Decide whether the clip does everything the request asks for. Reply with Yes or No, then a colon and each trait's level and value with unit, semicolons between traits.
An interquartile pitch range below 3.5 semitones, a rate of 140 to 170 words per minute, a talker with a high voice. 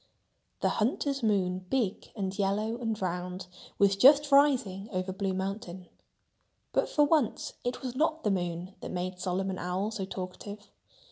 No: average, 4.1 semitones; average, 150 wpm; high, 195 Hz